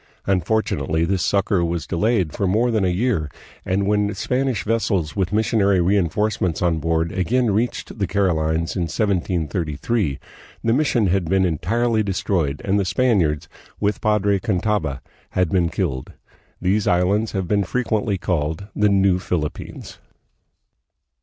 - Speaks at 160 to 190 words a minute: No, average, 145 wpm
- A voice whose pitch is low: Yes, very low, 95 Hz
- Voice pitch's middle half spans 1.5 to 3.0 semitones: No, average, 3.8 semitones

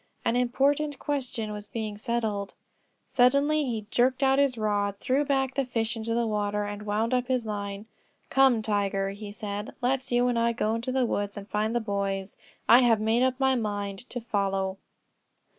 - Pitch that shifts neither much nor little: Yes, average, 3.6 semitones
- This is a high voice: Yes, high, 225 Hz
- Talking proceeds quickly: No, average, 185 wpm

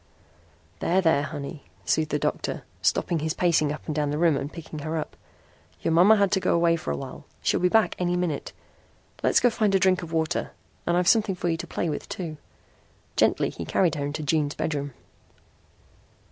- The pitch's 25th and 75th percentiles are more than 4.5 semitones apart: No, average, 3.0 semitones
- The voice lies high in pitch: No, medium, 165 Hz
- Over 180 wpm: Yes, average, 200 wpm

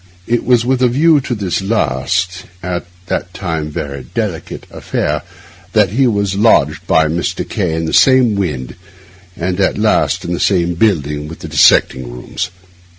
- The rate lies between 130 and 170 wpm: Yes, average, 155 wpm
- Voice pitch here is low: Yes, very low, 90 Hz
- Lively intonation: Yes, wide, 5.7 semitones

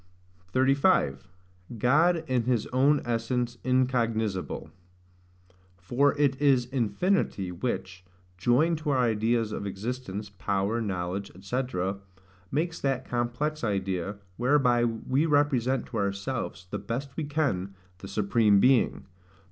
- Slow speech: Yes, slow, 115 wpm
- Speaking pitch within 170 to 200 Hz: No, low, 120 Hz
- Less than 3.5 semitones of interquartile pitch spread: No, average, 5.1 semitones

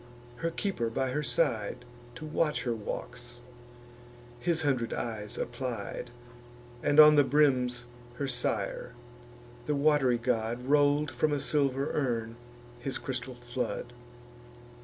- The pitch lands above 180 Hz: No, low, 125 Hz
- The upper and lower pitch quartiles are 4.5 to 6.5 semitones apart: No, average, 3.2 semitones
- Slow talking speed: Yes, slow, 120 wpm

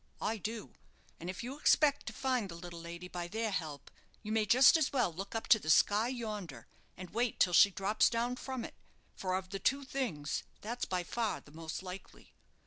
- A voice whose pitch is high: Yes, high, 205 Hz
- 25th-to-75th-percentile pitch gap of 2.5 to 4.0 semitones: No, average, 5.1 semitones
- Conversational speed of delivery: No, fast, 210 wpm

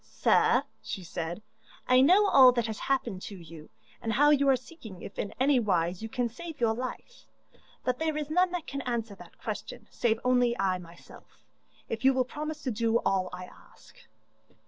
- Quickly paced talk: No, average, 190 wpm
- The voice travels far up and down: Yes, wide, 6.0 semitones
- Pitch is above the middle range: Yes, high, 240 Hz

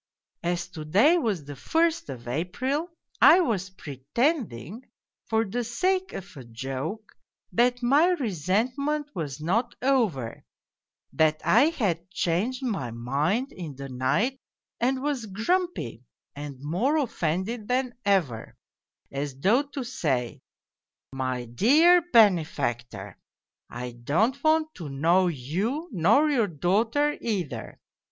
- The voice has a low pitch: No, high, 195 Hz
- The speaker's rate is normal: No, slow, 125 wpm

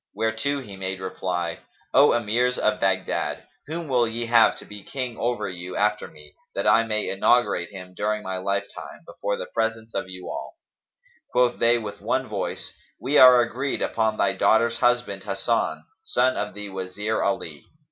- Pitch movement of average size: Yes, average, 3.7 semitones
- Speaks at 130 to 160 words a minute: No, average, 170 wpm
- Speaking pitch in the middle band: No, low, 110 Hz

